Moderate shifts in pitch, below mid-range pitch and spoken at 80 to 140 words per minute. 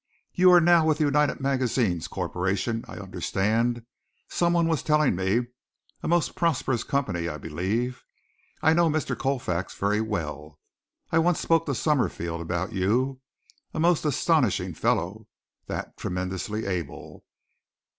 No: wide, 8.5 semitones; low, 120 Hz; slow, 135 wpm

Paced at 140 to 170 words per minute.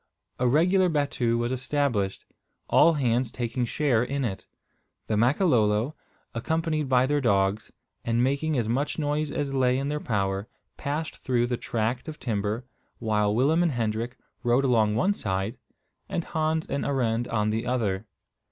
Yes: average, 155 wpm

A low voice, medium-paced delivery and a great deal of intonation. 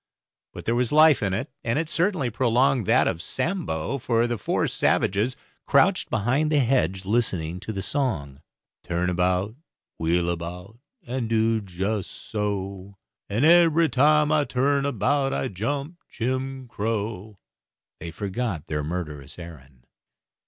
Yes: low, 110 Hz; average, 145 wpm; wide, 6.9 semitones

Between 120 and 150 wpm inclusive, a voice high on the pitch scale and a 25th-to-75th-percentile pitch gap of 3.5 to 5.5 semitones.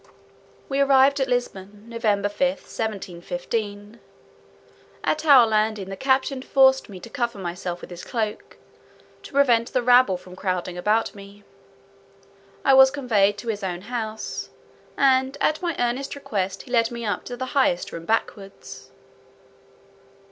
Yes: average, 145 wpm; high, 225 Hz; average, 4.8 semitones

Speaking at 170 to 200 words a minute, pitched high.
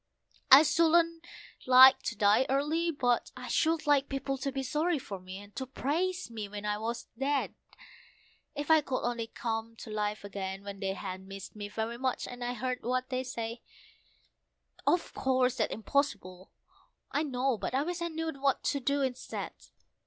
Yes: average, 180 wpm; very high, 255 Hz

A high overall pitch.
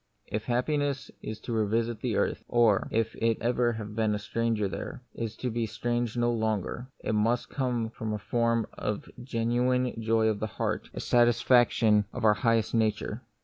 No: low, 115 Hz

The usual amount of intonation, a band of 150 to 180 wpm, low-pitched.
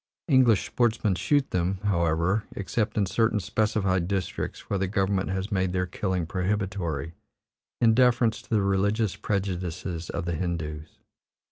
No: average, 3.3 semitones; average, 140 wpm; very low, 95 Hz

